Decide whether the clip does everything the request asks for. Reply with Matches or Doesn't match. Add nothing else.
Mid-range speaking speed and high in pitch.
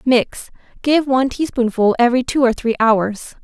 Matches